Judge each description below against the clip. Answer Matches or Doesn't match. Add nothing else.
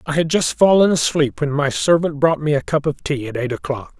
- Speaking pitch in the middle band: Matches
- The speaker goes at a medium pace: Doesn't match